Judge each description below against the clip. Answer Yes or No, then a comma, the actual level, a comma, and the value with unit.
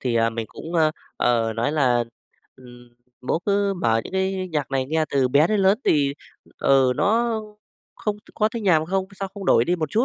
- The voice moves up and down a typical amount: No, wide, 7.4 semitones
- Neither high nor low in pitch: Yes, medium, 155 Hz